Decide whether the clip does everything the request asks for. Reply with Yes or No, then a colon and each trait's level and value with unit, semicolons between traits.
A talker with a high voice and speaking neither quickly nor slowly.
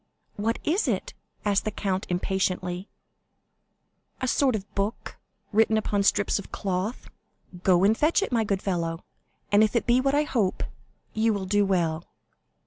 Yes: high, 205 Hz; average, 160 wpm